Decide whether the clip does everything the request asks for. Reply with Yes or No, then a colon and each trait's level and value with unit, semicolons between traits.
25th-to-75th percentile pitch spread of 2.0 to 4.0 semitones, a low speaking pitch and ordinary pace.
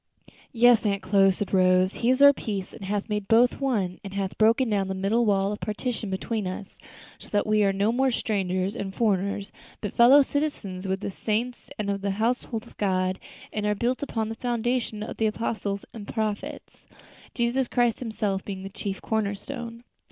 No: average, 3.3 semitones; high, 210 Hz; average, 195 wpm